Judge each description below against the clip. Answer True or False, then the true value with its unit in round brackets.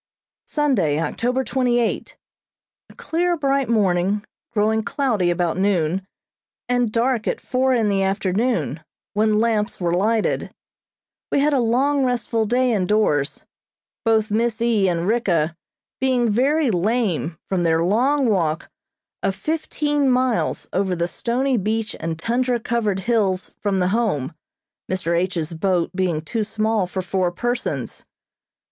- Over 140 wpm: False (135 wpm)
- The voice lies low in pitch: False (215 Hz)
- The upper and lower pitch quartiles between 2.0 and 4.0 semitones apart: False (5.0 semitones)